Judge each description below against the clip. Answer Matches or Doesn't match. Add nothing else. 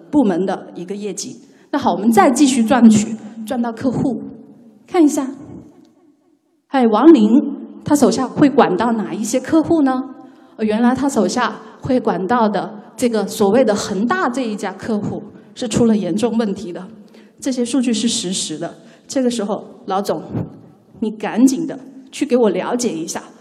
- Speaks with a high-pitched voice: Matches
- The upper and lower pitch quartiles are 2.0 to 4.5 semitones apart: Matches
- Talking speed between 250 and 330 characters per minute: Doesn't match